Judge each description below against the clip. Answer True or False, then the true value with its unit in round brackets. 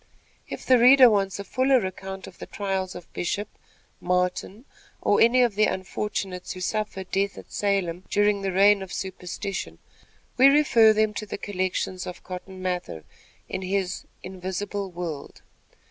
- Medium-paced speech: True (155 wpm)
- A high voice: True (195 Hz)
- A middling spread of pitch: False (2.3 semitones)